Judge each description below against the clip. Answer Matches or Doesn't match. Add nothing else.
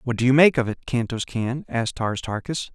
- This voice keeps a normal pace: Doesn't match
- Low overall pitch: Matches